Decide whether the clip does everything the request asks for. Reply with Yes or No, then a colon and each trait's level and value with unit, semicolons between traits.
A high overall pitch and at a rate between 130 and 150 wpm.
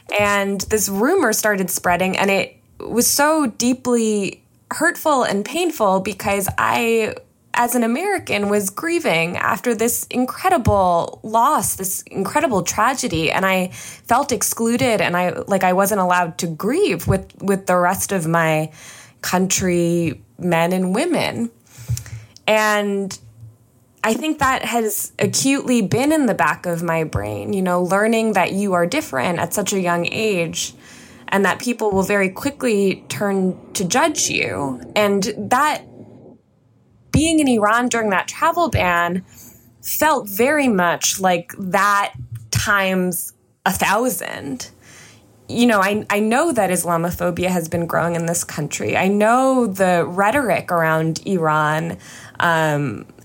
Yes: high, 195 Hz; slow, 135 wpm